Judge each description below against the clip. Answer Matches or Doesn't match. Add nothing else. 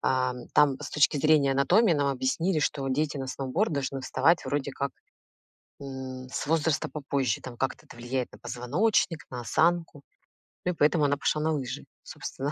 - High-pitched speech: Doesn't match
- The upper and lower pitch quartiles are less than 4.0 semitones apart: Matches